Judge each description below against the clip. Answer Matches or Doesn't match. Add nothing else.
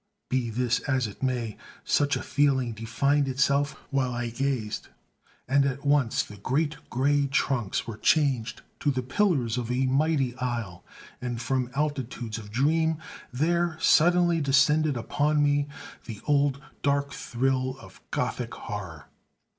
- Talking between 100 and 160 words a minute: Matches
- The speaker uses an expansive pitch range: Doesn't match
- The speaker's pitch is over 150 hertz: Doesn't match